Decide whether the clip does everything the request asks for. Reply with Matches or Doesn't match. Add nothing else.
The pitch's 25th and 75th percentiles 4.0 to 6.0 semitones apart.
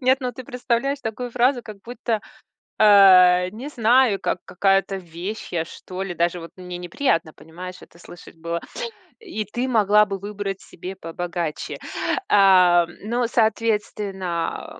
Matches